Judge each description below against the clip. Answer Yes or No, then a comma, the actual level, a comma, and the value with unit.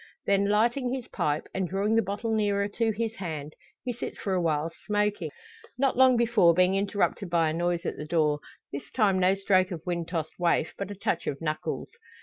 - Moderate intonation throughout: Yes, average, 4.0 semitones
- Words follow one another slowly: No, fast, 205 wpm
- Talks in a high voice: Yes, high, 195 Hz